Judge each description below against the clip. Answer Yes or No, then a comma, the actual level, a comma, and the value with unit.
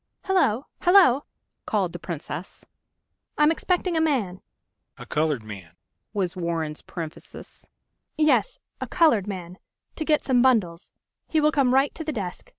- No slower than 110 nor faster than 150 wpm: Yes, average, 145 wpm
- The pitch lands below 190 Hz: No, high, 245 Hz